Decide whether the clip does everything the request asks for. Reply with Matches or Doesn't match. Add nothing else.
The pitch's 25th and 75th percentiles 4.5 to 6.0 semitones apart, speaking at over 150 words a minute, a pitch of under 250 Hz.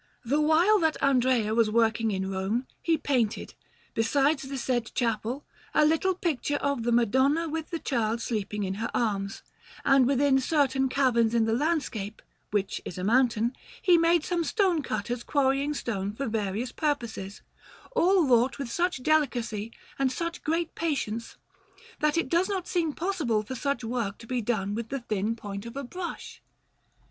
Doesn't match